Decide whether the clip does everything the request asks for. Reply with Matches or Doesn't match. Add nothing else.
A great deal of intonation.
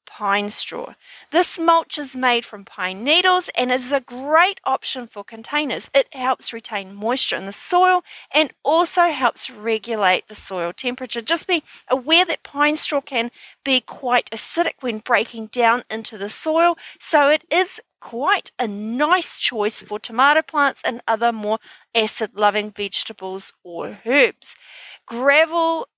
Matches